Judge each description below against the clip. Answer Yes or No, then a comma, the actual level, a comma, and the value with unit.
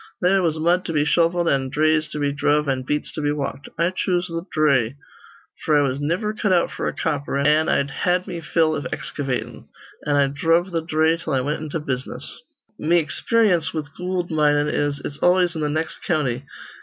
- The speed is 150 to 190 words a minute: No, fast, 205 wpm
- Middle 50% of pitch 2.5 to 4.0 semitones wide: Yes, average, 3.1 semitones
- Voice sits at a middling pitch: Yes, medium, 155 Hz